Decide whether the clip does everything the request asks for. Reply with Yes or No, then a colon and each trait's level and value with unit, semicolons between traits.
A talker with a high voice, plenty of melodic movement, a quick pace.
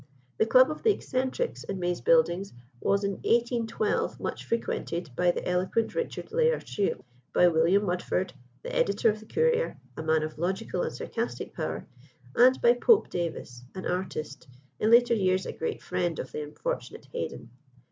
No: high, 195 Hz; wide, 5.7 semitones; average, 165 wpm